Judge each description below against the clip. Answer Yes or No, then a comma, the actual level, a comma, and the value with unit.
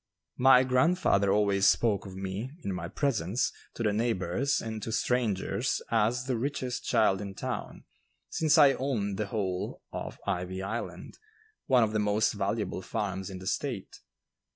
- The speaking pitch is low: Yes, low, 105 Hz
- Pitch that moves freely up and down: No, average, 4.3 semitones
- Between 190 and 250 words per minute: No, average, 155 wpm